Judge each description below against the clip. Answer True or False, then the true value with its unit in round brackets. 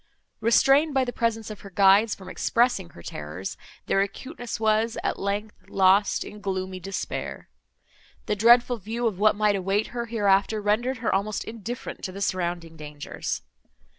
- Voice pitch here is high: True (210 Hz)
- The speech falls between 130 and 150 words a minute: False (160 wpm)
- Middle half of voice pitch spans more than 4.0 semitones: False (3.3 semitones)